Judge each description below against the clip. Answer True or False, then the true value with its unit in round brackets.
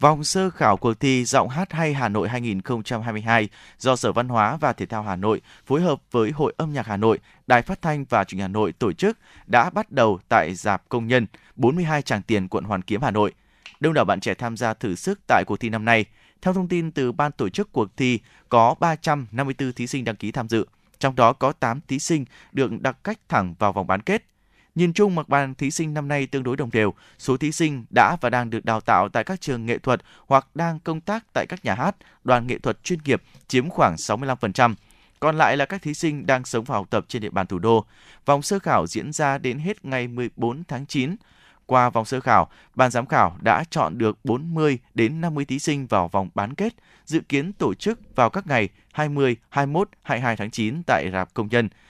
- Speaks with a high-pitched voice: False (125 Hz)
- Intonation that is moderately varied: True (5.0 semitones)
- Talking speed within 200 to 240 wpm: True (230 wpm)